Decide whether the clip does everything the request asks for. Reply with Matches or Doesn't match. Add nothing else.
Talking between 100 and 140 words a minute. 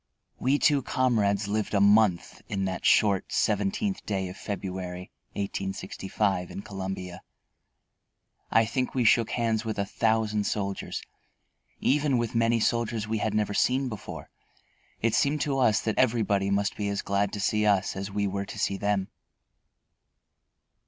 Doesn't match